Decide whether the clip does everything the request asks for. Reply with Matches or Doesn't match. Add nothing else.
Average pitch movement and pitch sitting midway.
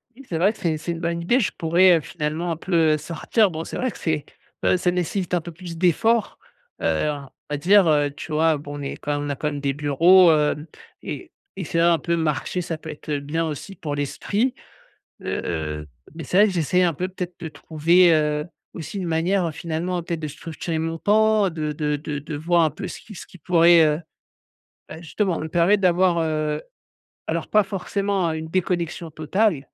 Matches